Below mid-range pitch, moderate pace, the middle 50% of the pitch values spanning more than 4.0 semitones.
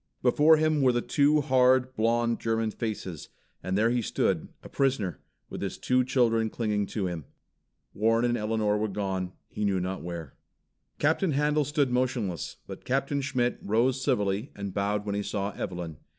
Yes: low, 115 Hz; average, 170 wpm; average, 4.4 semitones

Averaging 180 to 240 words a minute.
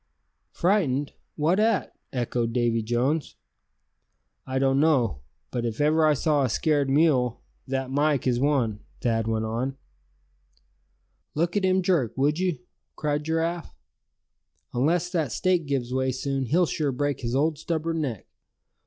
No: average, 145 wpm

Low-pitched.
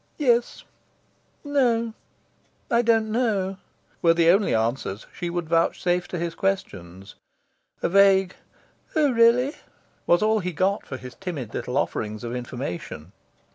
No: medium, 180 Hz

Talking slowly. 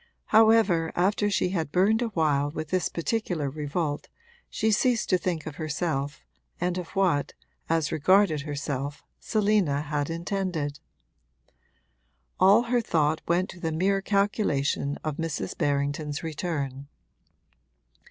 Yes: slow, 125 wpm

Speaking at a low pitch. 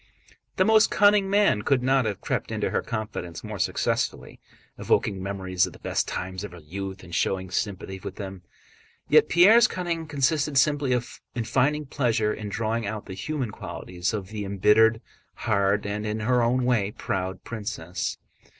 Yes: low, 110 Hz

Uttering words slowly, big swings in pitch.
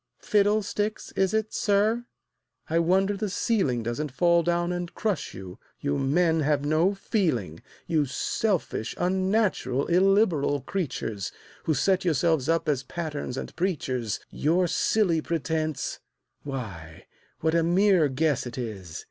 Yes: slow, 130 wpm; wide, 6.0 semitones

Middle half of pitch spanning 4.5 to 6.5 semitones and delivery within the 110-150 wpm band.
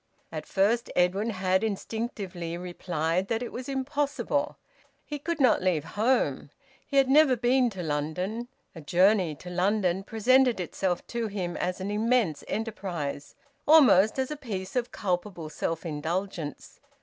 Yes: wide, 5.4 semitones; average, 145 wpm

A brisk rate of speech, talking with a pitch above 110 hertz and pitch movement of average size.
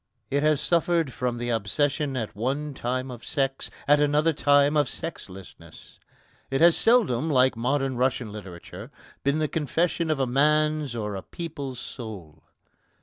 No: average, 150 wpm; low, 135 Hz; average, 4.0 semitones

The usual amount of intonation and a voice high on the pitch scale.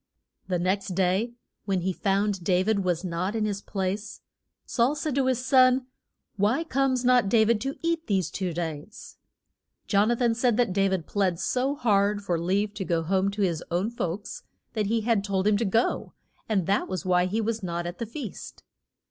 Yes: average, 4.0 semitones; high, 205 Hz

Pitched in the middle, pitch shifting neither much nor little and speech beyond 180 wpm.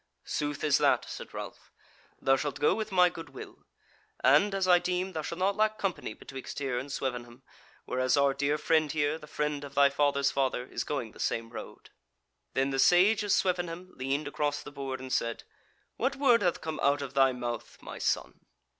Yes: medium, 145 Hz; average, 4.7 semitones; average, 200 wpm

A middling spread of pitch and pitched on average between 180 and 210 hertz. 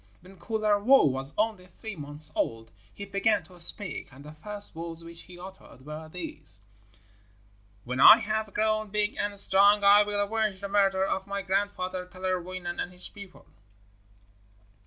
Yes: average, 3.3 semitones; high, 190 Hz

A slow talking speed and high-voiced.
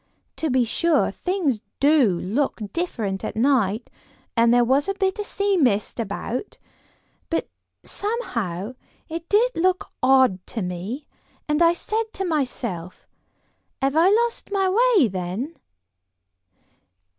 Yes: slow, 130 wpm; very high, 275 Hz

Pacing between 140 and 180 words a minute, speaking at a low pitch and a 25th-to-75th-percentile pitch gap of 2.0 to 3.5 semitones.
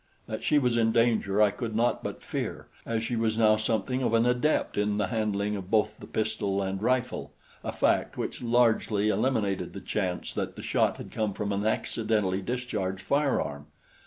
No: average, 190 wpm; low, 110 Hz; narrow, 2.6 semitones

